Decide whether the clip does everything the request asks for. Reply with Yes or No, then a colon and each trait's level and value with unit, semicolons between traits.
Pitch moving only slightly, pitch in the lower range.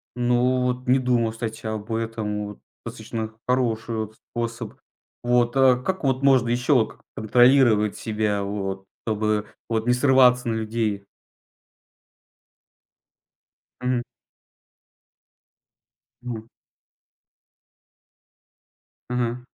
Yes: narrow, 2.3 semitones; low, 115 Hz